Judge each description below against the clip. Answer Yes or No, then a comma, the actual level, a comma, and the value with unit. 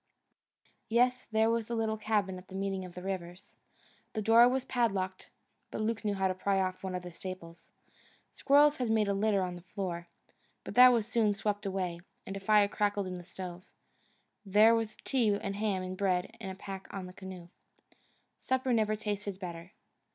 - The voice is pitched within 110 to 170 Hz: No, high, 200 Hz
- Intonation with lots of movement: No, average, 2.9 semitones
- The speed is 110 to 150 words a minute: No, average, 195 wpm